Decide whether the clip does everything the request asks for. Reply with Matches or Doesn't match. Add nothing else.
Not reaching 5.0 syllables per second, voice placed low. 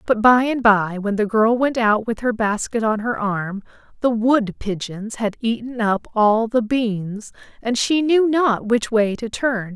Doesn't match